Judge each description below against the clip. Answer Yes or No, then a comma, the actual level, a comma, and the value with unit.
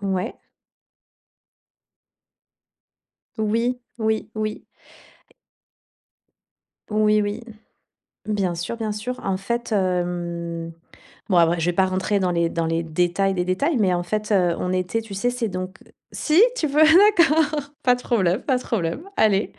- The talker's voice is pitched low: No, high, 200 Hz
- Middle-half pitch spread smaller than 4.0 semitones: No, average, 4.8 semitones